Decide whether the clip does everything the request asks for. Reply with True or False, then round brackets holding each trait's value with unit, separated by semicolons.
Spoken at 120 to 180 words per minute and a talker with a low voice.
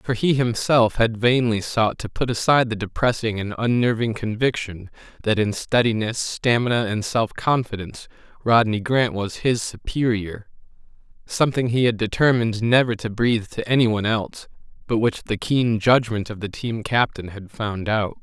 True (160 wpm; 115 Hz)